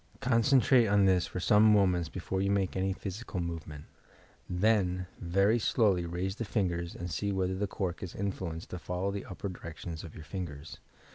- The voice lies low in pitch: Yes, very low, 95 Hz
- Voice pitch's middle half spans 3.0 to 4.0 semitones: No, narrow, 2.5 semitones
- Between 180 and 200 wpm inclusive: Yes, average, 185 wpm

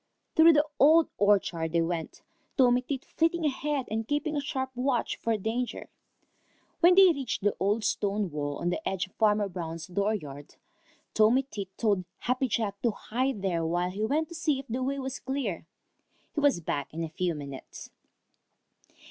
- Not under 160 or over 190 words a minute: Yes, average, 175 wpm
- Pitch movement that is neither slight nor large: No, wide, 7.1 semitones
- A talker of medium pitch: No, high, 220 Hz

